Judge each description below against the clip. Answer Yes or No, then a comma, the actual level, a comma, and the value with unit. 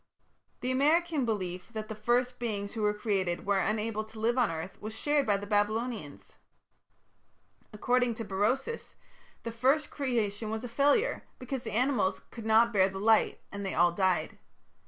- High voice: Yes, high, 220 Hz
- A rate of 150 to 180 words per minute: Yes, average, 170 wpm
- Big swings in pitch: No, average, 3.5 semitones